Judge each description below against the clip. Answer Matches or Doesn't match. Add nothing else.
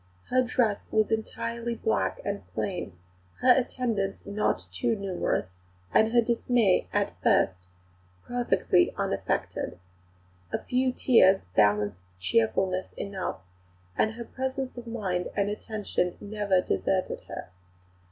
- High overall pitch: Matches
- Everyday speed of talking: Doesn't match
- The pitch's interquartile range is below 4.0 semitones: Doesn't match